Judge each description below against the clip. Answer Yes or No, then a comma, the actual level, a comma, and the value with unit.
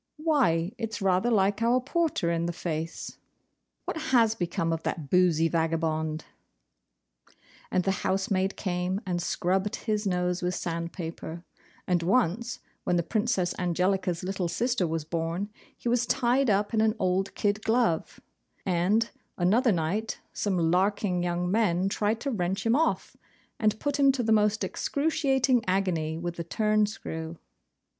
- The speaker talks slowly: No, average, 150 wpm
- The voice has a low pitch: No, high, 190 Hz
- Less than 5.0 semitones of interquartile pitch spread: Yes, average, 4.4 semitones